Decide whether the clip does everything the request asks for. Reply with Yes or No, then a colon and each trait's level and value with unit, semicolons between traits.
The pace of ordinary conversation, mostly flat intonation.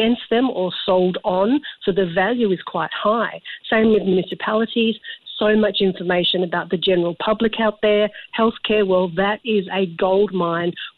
No: average, 165 wpm; average, 3.1 semitones